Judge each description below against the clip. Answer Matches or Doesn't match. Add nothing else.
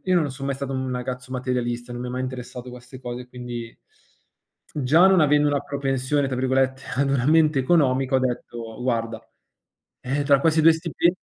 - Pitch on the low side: Matches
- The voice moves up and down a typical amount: Doesn't match